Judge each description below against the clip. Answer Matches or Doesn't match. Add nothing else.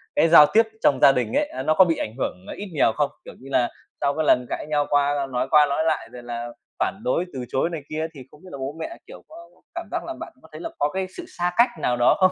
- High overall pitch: Doesn't match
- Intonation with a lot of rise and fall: Doesn't match